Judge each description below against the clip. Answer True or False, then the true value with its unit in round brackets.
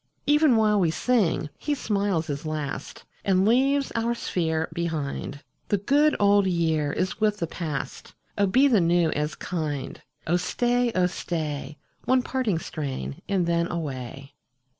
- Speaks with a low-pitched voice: False (175 Hz)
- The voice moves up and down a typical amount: False (5.9 semitones)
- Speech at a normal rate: True (155 wpm)